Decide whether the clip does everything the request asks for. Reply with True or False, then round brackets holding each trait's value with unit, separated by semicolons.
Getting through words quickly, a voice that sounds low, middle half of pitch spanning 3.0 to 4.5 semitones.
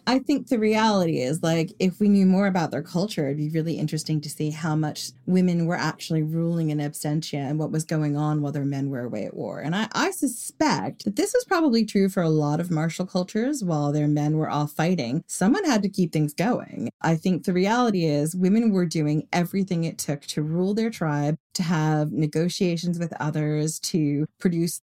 False (210 wpm; 165 Hz; 3.9 semitones)